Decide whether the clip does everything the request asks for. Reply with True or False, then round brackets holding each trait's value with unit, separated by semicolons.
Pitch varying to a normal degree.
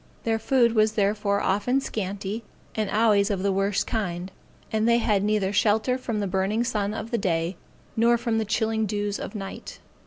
False (2.1 semitones)